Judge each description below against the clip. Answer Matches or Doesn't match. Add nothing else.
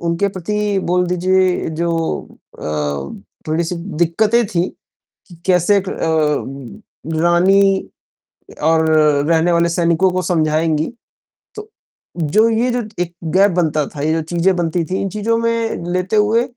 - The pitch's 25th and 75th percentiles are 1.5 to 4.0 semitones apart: Matches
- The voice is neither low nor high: Matches